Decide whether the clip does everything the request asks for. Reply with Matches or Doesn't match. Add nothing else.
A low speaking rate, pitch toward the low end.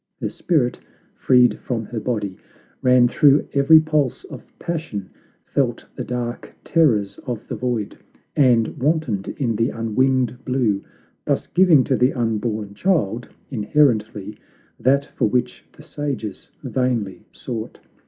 Matches